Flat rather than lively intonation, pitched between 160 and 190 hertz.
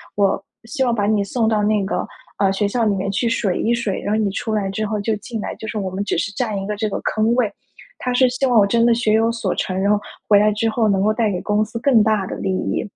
No: narrow, 2.3 semitones; high, 215 Hz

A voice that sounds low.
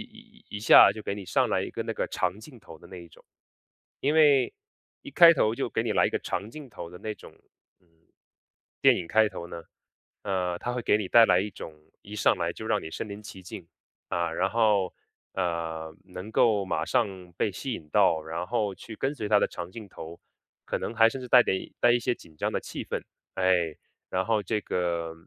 Yes: low, 100 Hz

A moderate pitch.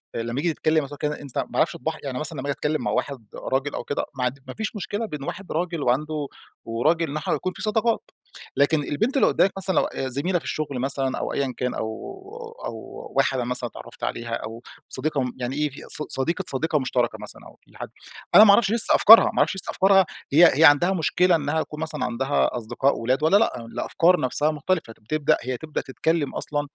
Yes: medium, 150 Hz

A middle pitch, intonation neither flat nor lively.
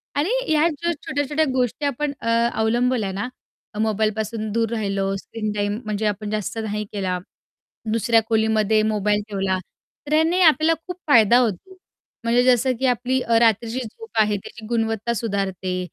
No: high, 225 Hz; average, 3.4 semitones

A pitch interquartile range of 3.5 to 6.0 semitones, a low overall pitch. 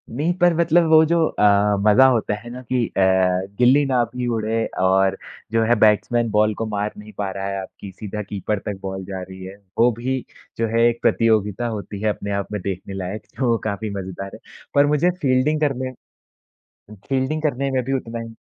Yes: average, 4.7 semitones; low, 110 Hz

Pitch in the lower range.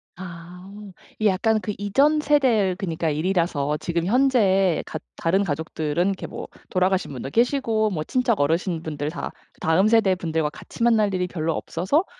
No: medium, 185 Hz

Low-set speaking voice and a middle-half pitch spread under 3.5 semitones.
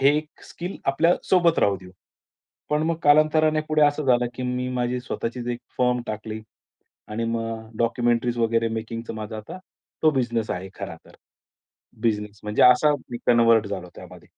No: low, 120 Hz; average, 4.6 semitones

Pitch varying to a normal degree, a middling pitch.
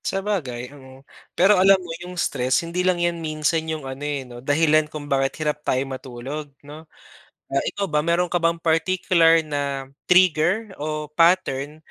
Yes: average, 3.6 semitones; medium, 155 Hz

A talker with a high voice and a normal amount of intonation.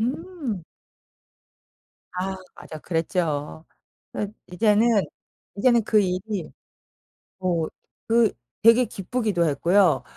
Yes: high, 200 Hz; average, 4.6 semitones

